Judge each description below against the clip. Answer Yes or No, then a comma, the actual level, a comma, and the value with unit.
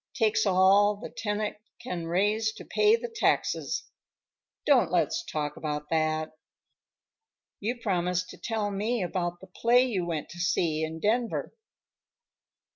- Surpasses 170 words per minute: No, slow, 135 wpm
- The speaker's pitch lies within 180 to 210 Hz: Yes, high, 190 Hz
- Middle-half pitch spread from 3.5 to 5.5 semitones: Yes, average, 4.5 semitones